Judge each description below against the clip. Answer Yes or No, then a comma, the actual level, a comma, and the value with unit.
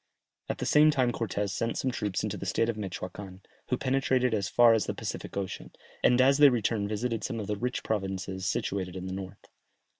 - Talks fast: Yes, fast, 210 wpm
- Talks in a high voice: No, low, 105 Hz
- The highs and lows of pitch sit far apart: No, average, 4.2 semitones